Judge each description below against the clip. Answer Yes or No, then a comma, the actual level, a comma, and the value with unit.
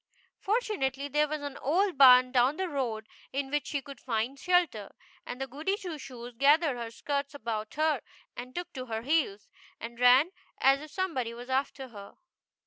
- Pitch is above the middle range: Yes, very high, 270 Hz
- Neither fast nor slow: Yes, average, 180 wpm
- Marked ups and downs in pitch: No, average, 3.8 semitones